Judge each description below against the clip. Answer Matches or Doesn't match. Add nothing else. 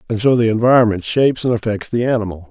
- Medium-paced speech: Doesn't match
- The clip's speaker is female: Doesn't match